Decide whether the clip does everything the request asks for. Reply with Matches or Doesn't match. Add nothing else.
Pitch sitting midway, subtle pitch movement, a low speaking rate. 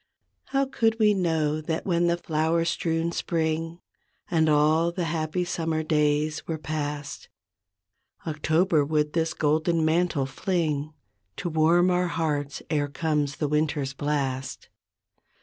Matches